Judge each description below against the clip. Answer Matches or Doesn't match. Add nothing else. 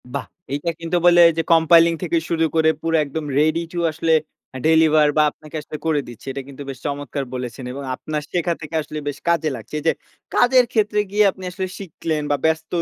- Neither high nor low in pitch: Matches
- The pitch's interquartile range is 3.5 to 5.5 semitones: Doesn't match